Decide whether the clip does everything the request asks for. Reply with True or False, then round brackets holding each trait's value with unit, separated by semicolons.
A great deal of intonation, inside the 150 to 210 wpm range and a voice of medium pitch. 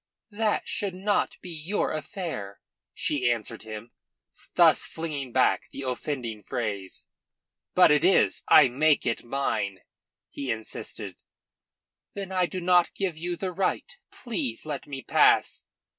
False (7.2 semitones; 135 wpm; 150 Hz)